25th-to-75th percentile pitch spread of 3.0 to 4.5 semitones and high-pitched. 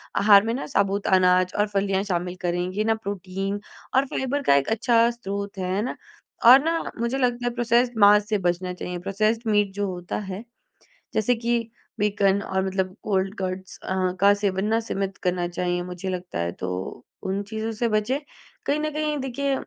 Yes: average, 3.7 semitones; high, 200 Hz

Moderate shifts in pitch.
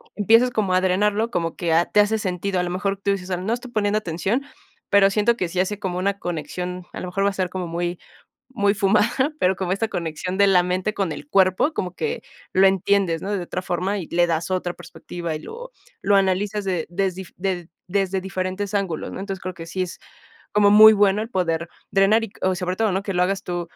No: narrow, 2.2 semitones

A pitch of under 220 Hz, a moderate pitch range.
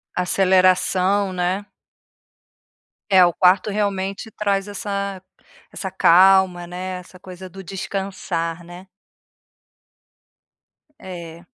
No: medium, 185 Hz; narrow, 1.6 semitones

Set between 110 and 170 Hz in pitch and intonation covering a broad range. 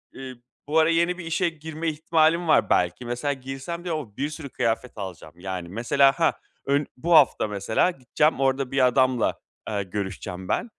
Yes: low, 135 Hz; wide, 5.9 semitones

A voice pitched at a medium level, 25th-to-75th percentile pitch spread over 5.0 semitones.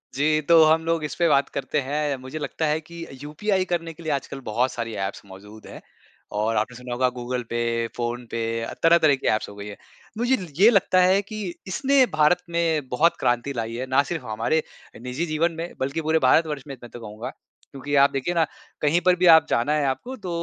Yes: medium, 145 Hz; wide, 5.4 semitones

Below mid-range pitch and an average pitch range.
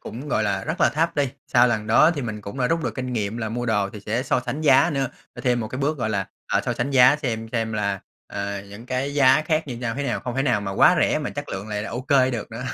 Yes: low, 120 Hz; average, 4.0 semitones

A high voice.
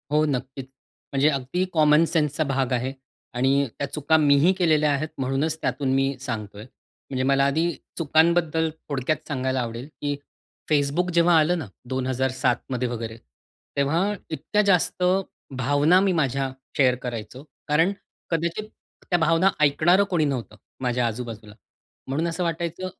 No: medium, 145 Hz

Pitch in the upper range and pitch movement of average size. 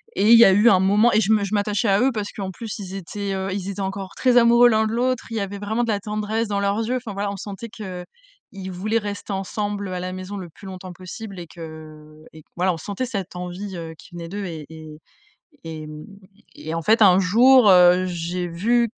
Yes: high, 195 Hz; average, 3.2 semitones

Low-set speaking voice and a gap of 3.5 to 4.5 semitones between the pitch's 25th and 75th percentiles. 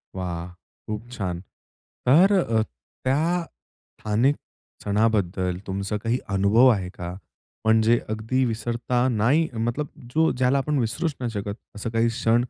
Yes: low, 115 Hz; average, 3.8 semitones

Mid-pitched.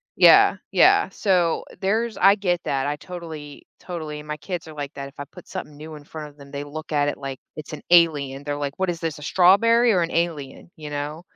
Yes: medium, 155 Hz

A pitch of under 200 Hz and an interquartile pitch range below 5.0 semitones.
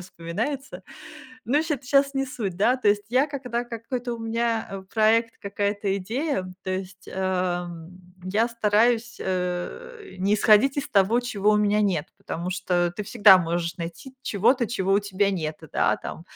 No: high, 210 Hz; average, 4.4 semitones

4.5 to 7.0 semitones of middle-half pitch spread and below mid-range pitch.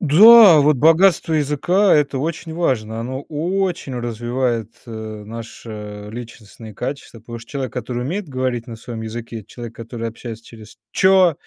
Yes: average, 5.2 semitones; low, 125 Hz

